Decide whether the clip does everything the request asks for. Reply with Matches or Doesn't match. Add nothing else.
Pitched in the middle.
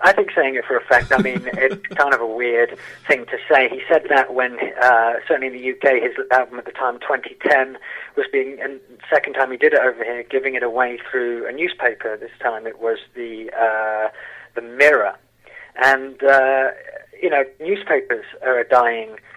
Doesn't match